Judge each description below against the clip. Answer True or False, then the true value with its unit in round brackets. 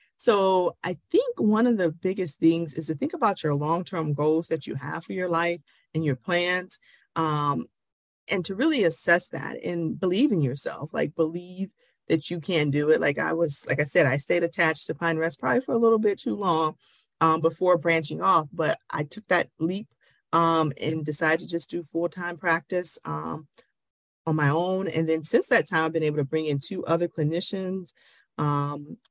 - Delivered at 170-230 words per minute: True (200 wpm)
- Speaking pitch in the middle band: True (165 Hz)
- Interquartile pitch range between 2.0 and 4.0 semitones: True (2.4 semitones)